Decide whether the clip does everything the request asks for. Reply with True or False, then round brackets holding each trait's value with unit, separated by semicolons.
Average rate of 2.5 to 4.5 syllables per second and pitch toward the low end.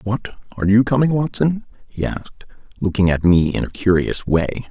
False (5.3 syllables/s; 110 Hz)